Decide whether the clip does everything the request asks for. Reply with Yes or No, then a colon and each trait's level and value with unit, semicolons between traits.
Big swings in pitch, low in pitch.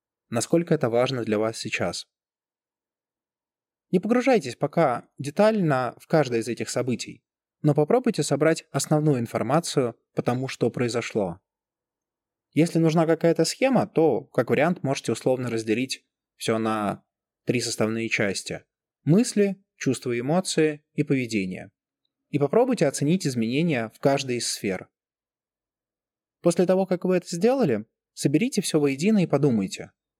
No: wide, 6.1 semitones; medium, 145 Hz